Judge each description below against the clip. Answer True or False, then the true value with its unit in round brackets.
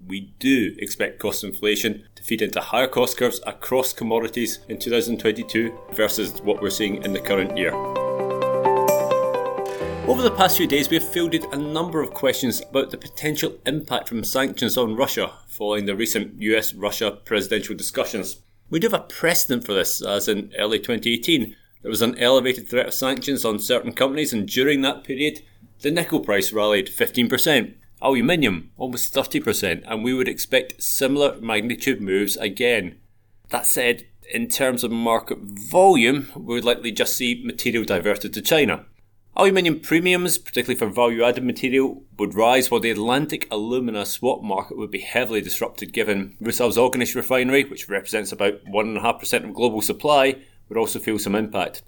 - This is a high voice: False (120 Hz)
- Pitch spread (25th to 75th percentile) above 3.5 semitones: True (4.4 semitones)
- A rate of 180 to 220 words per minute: False (165 wpm)